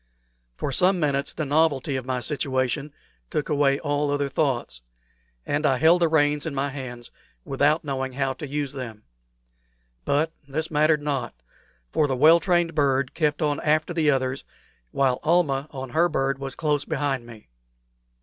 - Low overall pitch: No, medium, 145 Hz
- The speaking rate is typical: Yes, average, 165 wpm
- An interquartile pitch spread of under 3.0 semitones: Yes, narrow, 2.5 semitones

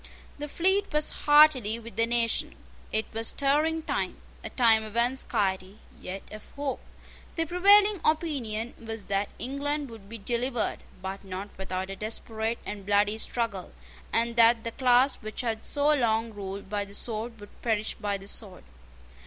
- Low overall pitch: No, high, 230 Hz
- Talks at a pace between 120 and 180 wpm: Yes, average, 165 wpm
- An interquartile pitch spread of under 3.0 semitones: No, average, 4.7 semitones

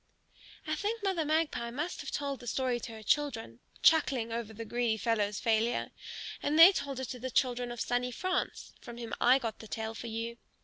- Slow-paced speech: No, fast, 205 wpm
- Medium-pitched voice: No, high, 245 Hz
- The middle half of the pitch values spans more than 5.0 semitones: No, average, 4.1 semitones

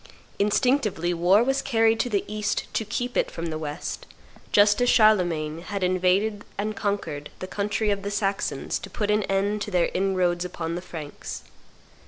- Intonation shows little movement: No, average, 3.3 semitones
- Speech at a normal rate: Yes, average, 175 wpm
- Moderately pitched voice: No, high, 200 Hz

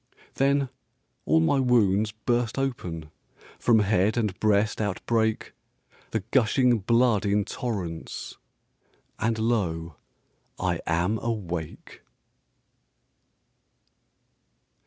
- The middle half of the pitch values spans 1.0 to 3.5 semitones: No, average, 4.3 semitones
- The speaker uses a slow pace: Yes, slow, 85 wpm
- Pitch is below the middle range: Yes, low, 110 Hz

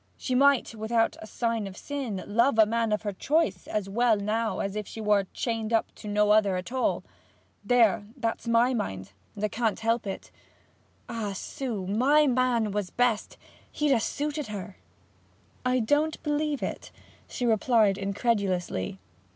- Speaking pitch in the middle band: No, high, 225 Hz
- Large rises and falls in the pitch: No, average, 3.3 semitones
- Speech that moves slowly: No, average, 165 wpm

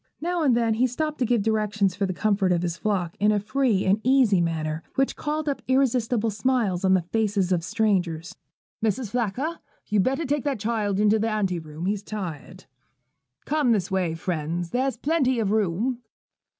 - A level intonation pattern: No, average, 5.2 semitones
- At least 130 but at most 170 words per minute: No, average, 185 wpm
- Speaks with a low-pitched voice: No, high, 215 Hz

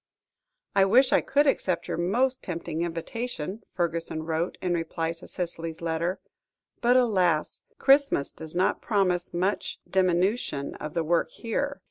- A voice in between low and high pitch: Yes, medium, 175 Hz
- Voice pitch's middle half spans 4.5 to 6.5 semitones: Yes, average, 5.2 semitones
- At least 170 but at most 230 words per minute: No, average, 140 wpm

